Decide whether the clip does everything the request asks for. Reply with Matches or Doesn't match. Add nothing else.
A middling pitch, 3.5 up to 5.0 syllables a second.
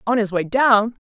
Doesn't match